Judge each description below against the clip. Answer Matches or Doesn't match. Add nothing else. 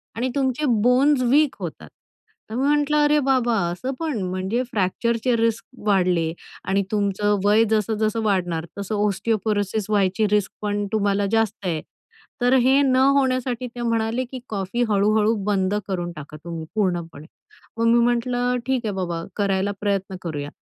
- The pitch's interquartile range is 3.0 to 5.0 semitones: Matches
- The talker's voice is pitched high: Matches